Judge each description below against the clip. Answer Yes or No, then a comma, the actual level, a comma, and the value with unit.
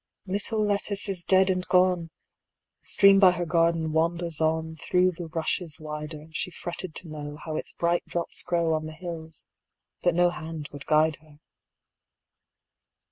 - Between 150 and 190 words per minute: No, slow, 135 wpm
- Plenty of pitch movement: No, narrow, 2.4 semitones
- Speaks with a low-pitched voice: No, medium, 165 Hz